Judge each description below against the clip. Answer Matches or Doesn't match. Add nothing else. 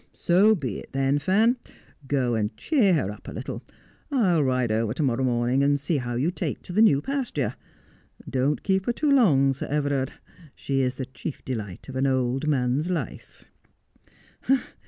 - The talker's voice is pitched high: Doesn't match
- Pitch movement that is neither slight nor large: Doesn't match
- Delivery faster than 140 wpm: Matches